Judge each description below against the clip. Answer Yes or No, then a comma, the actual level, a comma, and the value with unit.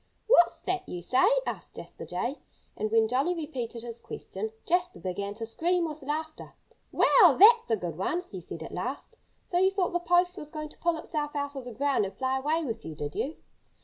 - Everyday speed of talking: No, fast, 210 wpm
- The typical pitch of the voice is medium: No, very high, 285 Hz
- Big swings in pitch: Yes, wide, 7.4 semitones